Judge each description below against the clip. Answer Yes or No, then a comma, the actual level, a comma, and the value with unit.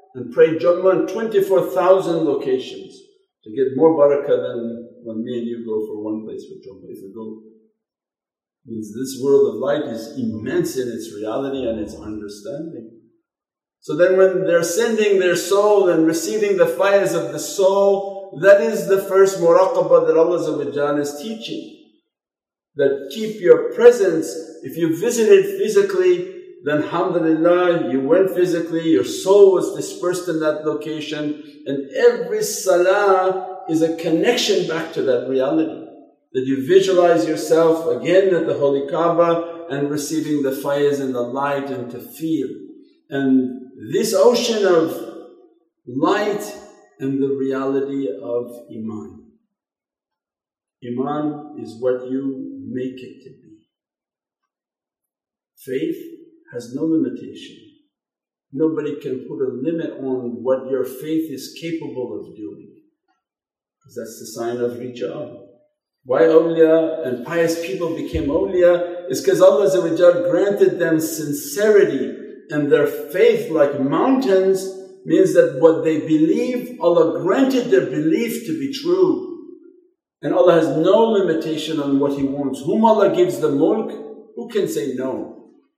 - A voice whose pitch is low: No, medium, 175 Hz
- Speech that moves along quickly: No, average, 140 wpm